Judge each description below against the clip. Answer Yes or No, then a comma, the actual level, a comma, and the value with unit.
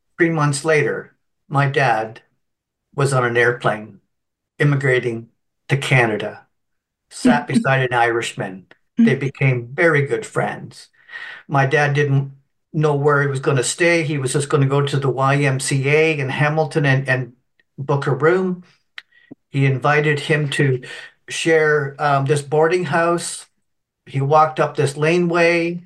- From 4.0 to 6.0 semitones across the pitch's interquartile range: No, average, 3.0 semitones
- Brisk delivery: No, average, 140 wpm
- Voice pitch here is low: No, medium, 145 Hz